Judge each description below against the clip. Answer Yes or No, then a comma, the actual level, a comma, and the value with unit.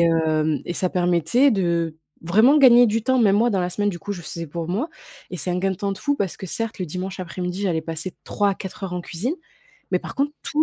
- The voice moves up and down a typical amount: Yes, average, 4.1 semitones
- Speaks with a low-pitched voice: No, medium, 185 Hz